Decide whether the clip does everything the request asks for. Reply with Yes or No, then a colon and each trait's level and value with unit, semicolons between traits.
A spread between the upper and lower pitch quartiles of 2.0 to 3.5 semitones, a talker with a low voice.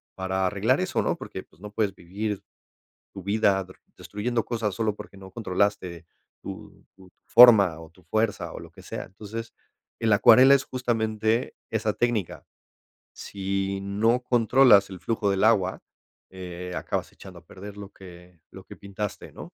Yes: average, 2.8 semitones; low, 100 Hz